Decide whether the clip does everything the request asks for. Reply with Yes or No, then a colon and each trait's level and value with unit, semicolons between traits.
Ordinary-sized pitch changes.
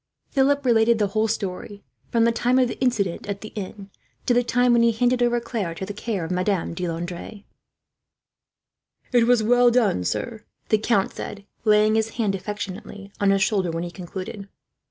Yes: average, 3.3 semitones